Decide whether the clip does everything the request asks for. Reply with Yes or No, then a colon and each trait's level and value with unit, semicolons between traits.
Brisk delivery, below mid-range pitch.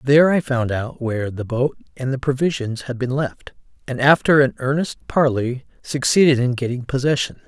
No: average, 175 wpm; low, 130 Hz